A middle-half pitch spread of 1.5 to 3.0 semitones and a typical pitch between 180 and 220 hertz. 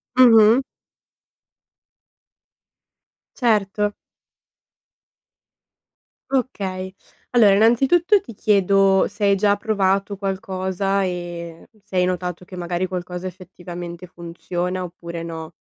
Yes: average, 2.7 semitones; high, 190 Hz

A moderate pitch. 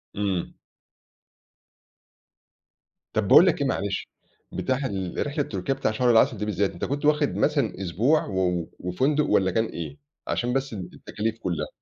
No: low, 110 Hz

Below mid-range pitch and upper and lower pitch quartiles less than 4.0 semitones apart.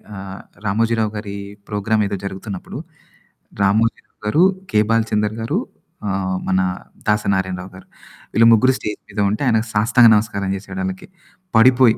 Yes: low, 105 Hz; narrow, 2.5 semitones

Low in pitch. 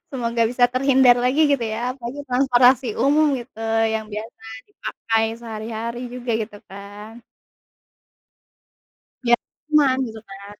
No: high, 240 Hz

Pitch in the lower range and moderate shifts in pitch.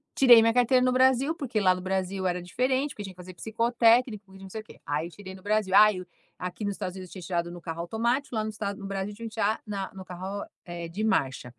No: high, 200 Hz; average, 3.8 semitones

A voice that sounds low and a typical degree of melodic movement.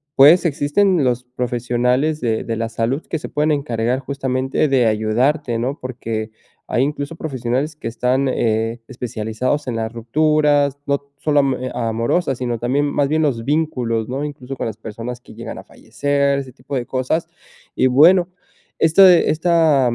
Yes: low, 130 Hz; average, 3.6 semitones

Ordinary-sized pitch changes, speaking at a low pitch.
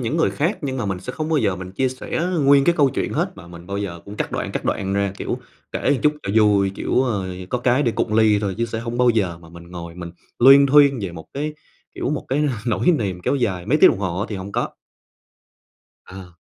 No: wide, 6.2 semitones; low, 110 Hz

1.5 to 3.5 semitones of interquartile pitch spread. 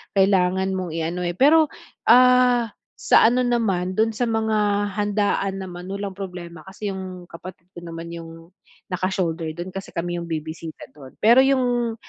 No: average, 4.2 semitones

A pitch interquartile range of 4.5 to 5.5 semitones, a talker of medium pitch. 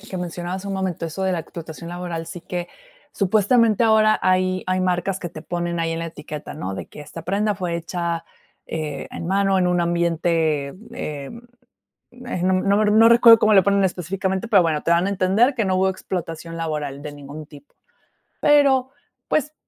No: average, 3.1 semitones; medium, 180 Hz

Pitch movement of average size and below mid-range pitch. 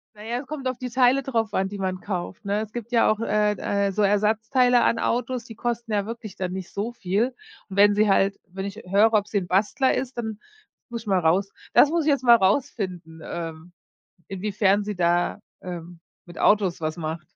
No: average, 3.9 semitones; high, 205 Hz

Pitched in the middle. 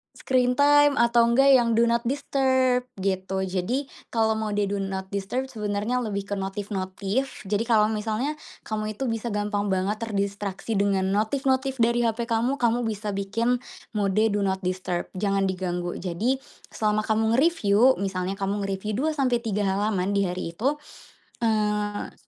No: high, 210 Hz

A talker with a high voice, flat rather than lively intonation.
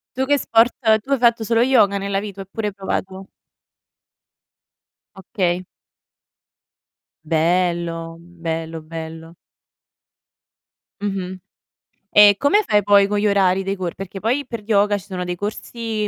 No: high, 200 Hz; average, 3.5 semitones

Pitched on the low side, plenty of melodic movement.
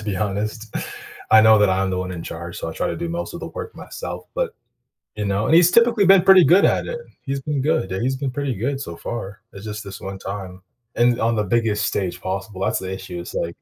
Yes: low, 110 Hz; wide, 6.9 semitones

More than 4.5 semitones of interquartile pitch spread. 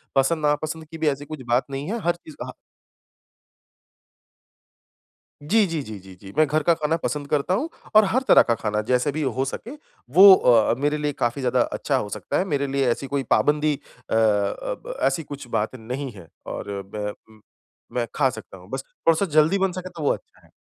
Yes: average, 4.9 semitones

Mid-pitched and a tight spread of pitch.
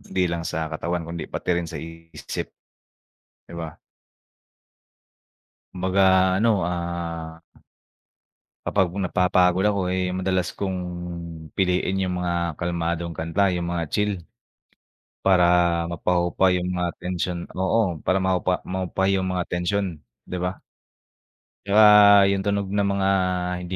No: very low, 90 Hz; narrow, 1.9 semitones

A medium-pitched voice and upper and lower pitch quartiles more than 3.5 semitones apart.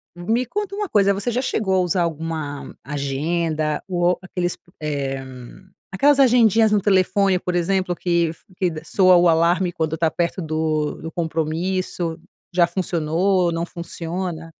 No: medium, 175 Hz; average, 2.9 semitones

